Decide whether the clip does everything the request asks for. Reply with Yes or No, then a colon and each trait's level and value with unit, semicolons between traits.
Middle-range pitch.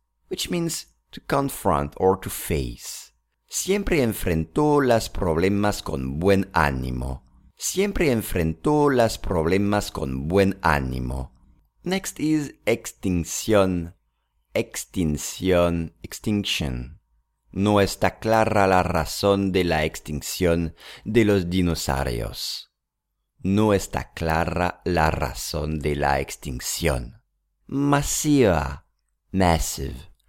No: very low, 85 Hz